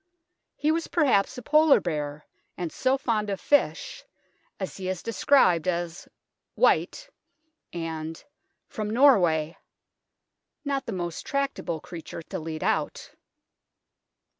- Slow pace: Yes, slow, 130 wpm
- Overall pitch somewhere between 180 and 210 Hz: Yes, high, 190 Hz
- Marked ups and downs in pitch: Yes, wide, 8.7 semitones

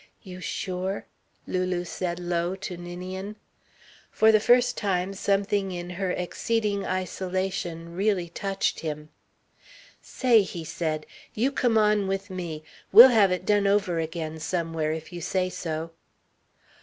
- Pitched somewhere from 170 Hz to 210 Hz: Yes, medium, 185 Hz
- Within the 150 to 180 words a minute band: No, slow, 135 wpm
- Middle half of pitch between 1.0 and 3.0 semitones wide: Yes, average, 2.7 semitones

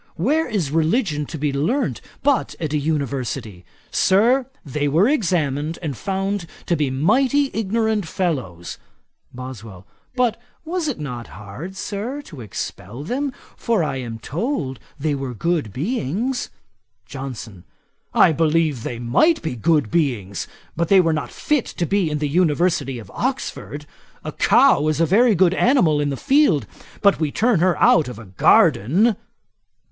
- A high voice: No, medium, 160 Hz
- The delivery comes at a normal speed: Yes, average, 155 wpm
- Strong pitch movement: Yes, wide, 7.2 semitones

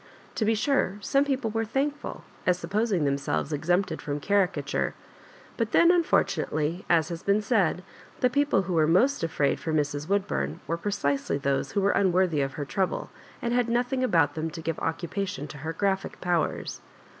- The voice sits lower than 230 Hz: Yes, medium, 185 Hz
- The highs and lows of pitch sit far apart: Yes, wide, 5.7 semitones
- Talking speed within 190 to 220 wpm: No, average, 180 wpm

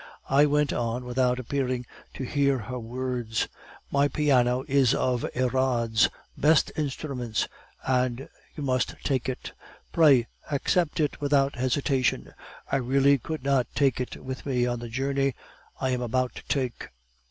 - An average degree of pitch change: No, narrow, 2.1 semitones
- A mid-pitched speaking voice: No, low, 130 Hz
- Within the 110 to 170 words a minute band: Yes, average, 150 wpm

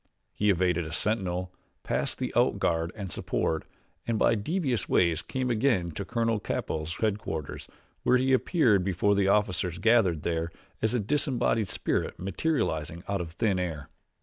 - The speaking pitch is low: Yes, low, 100 Hz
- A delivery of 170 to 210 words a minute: No, average, 155 wpm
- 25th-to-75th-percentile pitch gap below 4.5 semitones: No, average, 4.9 semitones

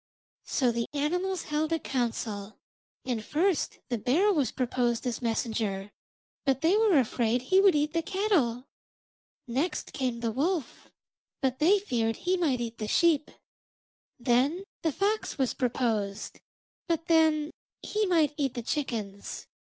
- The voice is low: No, very high, 270 Hz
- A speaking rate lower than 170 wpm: Yes, average, 145 wpm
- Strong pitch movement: Yes, wide, 5.9 semitones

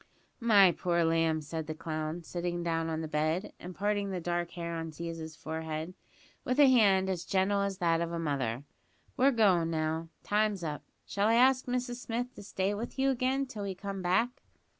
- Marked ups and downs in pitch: No, average, 4.4 semitones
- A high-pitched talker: No, medium, 180 Hz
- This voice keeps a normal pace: Yes, average, 195 wpm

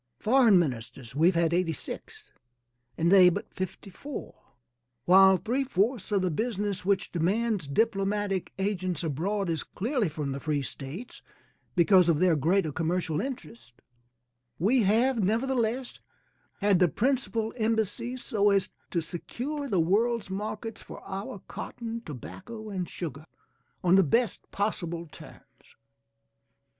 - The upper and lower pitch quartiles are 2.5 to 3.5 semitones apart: No, average, 4.8 semitones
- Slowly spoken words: Yes, slow, 130 wpm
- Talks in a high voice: Yes, high, 195 Hz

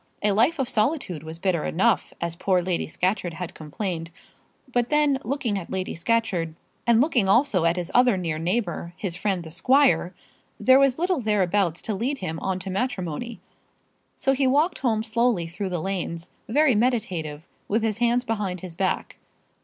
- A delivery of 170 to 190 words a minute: Yes, average, 175 wpm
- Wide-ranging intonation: Yes, wide, 5.8 semitones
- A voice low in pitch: No, high, 200 Hz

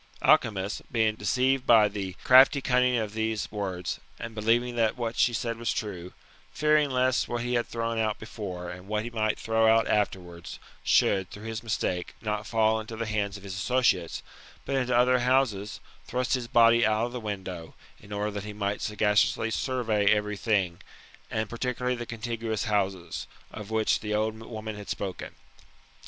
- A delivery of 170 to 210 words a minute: Yes, average, 175 wpm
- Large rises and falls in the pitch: No, narrow, 2.5 semitones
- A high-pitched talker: No, low, 110 Hz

